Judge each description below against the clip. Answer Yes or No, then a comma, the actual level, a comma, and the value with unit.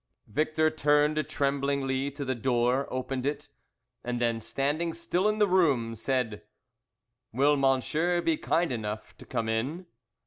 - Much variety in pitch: No, average, 4.2 semitones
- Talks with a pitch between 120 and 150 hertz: Yes, medium, 140 Hz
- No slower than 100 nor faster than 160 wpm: Yes, average, 140 wpm